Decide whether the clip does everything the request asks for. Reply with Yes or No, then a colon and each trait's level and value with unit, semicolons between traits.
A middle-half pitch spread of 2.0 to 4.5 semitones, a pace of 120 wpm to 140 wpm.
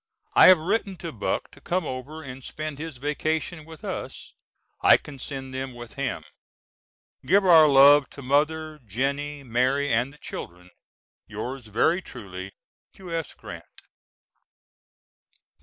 Yes: average, 3.9 semitones; slow, 135 wpm